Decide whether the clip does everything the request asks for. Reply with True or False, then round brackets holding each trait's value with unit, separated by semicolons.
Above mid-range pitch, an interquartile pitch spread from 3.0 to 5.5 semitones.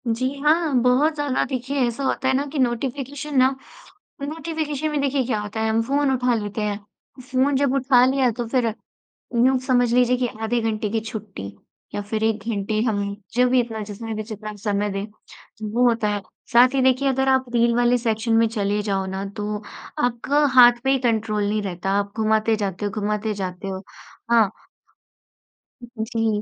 True (230 Hz; 3.6 semitones)